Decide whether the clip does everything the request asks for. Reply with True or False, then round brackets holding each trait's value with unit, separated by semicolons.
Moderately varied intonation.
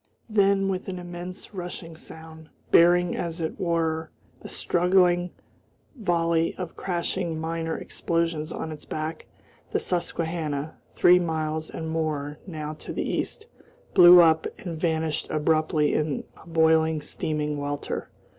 False (1.9 semitones)